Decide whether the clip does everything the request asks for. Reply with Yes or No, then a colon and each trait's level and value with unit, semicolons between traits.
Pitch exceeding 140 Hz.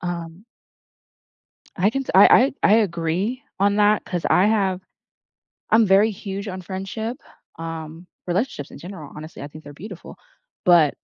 Yes: high, 190 Hz